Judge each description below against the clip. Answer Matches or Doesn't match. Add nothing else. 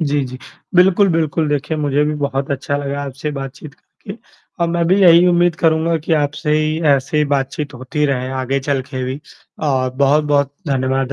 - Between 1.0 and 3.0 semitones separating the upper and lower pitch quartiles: Matches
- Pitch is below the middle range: Doesn't match